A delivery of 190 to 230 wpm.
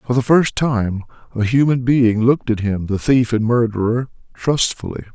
No: average, 175 wpm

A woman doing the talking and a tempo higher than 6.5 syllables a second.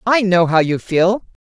No: female; 4.3 syllables/s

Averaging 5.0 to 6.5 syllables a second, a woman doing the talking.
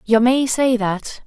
No: 3.5 syllables/s; female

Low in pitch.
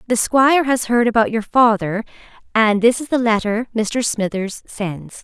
No: high, 225 Hz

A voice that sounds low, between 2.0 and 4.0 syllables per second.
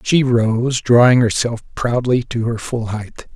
Yes: low, 120 Hz; 3.7 syllables/s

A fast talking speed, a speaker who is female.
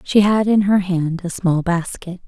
Yes: fast, 210 wpm; female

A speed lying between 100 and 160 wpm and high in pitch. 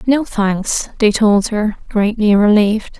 Yes: average, 140 wpm; high, 210 Hz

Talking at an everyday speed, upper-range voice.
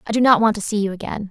No: fast, 365 wpm; high, 210 Hz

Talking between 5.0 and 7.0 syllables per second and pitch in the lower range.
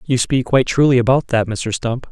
Yes: 5.5 syllables/s; low, 125 Hz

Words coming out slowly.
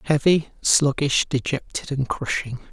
Yes: slow, 110 wpm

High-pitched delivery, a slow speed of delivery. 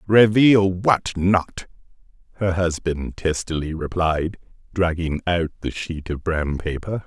No: very low, 90 Hz; slow, 120 wpm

